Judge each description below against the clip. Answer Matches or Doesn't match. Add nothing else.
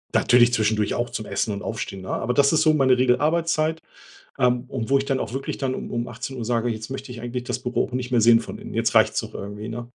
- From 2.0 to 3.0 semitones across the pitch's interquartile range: Matches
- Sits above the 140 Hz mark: Doesn't match